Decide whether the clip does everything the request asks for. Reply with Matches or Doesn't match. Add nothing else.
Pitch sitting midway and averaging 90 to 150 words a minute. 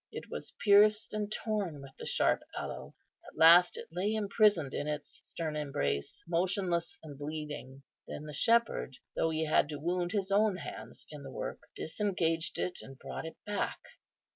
Doesn't match